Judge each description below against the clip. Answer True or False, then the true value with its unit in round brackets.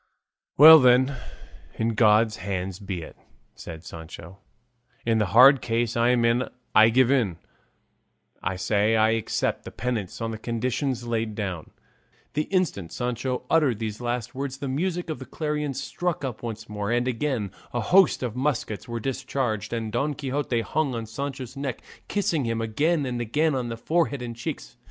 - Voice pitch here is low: True (120 Hz)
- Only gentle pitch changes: False (3.8 semitones)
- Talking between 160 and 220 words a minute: True (170 wpm)